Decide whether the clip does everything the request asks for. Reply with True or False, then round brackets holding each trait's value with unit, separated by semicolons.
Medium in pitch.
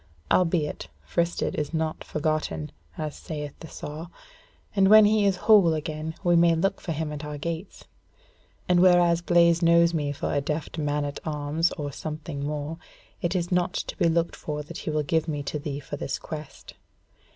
True (160 Hz)